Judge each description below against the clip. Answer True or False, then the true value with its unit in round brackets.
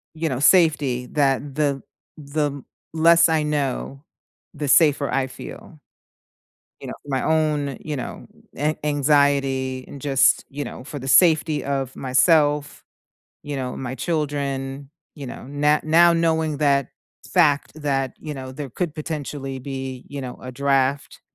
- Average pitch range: False (2.2 semitones)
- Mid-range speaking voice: True (145 Hz)